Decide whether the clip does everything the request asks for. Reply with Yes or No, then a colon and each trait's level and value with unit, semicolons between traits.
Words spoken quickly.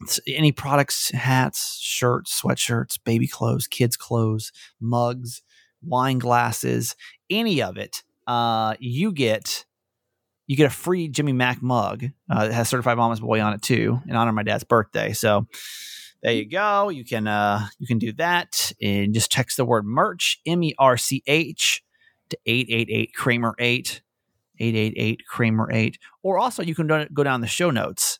No: average, 170 wpm